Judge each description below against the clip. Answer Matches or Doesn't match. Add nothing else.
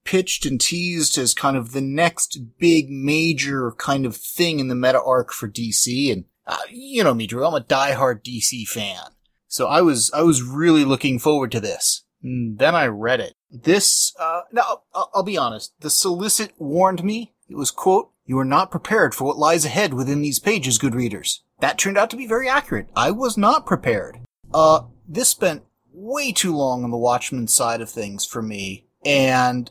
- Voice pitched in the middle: Matches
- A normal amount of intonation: Doesn't match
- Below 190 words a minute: Doesn't match